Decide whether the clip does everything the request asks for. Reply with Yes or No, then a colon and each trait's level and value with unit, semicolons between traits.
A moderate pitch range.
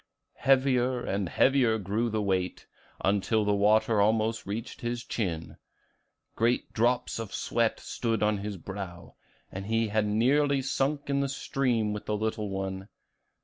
Yes: average, 3.1 semitones